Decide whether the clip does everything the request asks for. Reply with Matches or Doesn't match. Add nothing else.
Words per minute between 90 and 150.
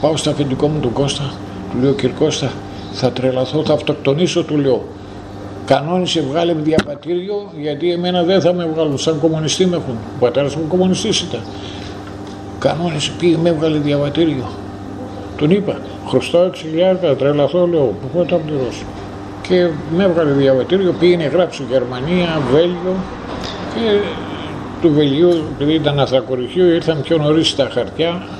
Matches